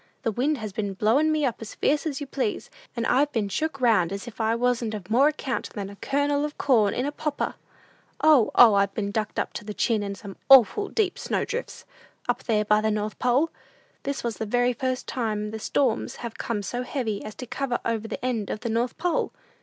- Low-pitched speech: No, high, 235 Hz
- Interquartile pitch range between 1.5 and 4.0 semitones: No, average, 4.5 semitones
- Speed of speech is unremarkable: No, fast, 230 wpm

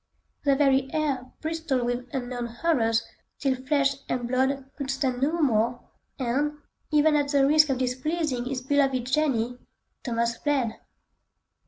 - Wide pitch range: No, average, 2.8 semitones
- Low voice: No, very high, 265 Hz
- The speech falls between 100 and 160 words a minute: Yes, average, 140 wpm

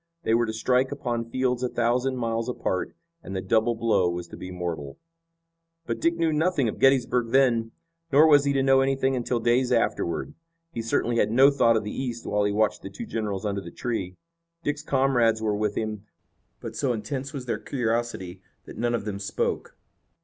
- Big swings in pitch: No, average, 3.8 semitones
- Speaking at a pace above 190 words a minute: Yes, average, 200 wpm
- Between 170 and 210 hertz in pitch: No, low, 120 Hz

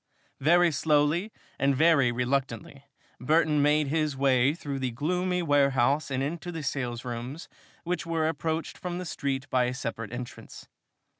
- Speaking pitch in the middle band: Yes, medium, 145 Hz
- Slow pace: No, average, 145 wpm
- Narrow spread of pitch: No, average, 3.8 semitones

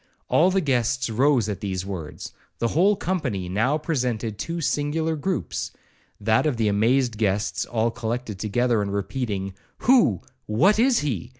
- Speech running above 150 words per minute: No, average, 145 wpm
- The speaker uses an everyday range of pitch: No, wide, 6.2 semitones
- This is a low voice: Yes, low, 120 Hz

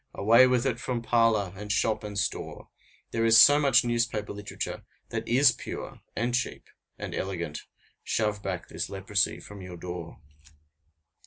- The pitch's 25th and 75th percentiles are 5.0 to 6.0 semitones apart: No, average, 3.3 semitones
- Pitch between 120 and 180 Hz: No, low, 110 Hz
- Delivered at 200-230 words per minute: No, average, 155 wpm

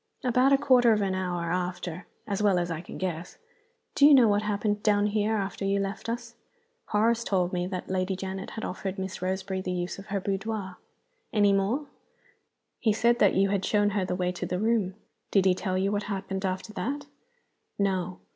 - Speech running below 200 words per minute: No, fast, 205 wpm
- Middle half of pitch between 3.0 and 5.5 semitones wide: No, narrow, 2.4 semitones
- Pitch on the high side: Yes, high, 195 Hz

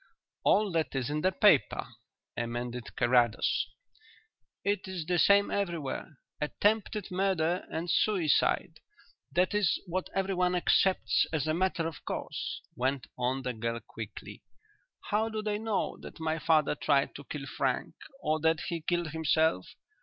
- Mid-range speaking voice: Yes, medium, 165 Hz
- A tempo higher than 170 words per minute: No, average, 145 wpm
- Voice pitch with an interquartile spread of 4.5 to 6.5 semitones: Yes, average, 5.0 semitones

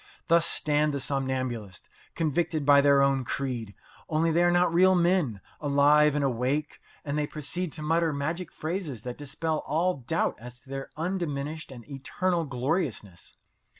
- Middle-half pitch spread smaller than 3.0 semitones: No, average, 3.5 semitones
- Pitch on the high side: No, medium, 150 Hz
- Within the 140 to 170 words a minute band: Yes, average, 155 wpm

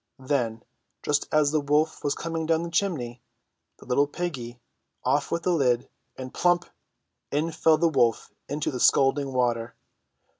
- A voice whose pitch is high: No, medium, 145 Hz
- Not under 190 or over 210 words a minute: No, average, 155 wpm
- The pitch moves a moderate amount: Yes, average, 4.4 semitones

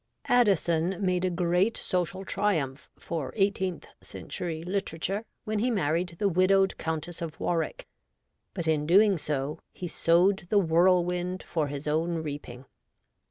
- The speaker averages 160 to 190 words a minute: No, slow, 135 wpm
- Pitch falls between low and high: Yes, medium, 175 Hz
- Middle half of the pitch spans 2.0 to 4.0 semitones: Yes, average, 3.1 semitones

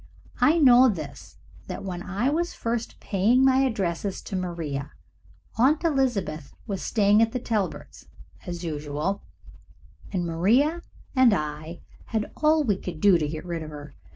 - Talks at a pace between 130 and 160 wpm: Yes, average, 155 wpm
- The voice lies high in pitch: Yes, high, 195 Hz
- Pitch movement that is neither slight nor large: No, wide, 7.1 semitones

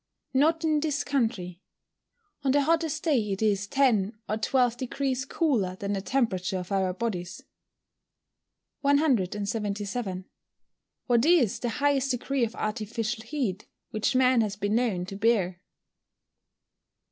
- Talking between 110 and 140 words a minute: Yes, slow, 135 wpm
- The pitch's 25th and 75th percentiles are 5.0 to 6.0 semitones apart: Yes, wide, 5.4 semitones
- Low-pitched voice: No, high, 230 Hz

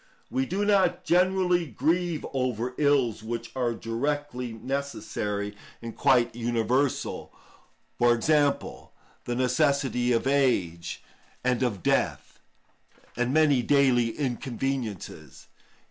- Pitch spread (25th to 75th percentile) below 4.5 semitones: Yes, average, 3.7 semitones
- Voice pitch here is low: Yes, low, 125 Hz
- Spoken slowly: Yes, slow, 100 wpm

